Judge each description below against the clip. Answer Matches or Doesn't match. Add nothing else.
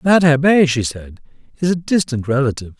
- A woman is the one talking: Doesn't match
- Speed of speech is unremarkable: Matches